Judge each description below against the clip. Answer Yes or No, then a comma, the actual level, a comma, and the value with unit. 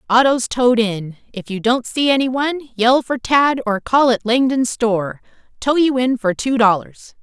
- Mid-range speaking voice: No, high, 240 Hz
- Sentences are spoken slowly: No, average, 200 wpm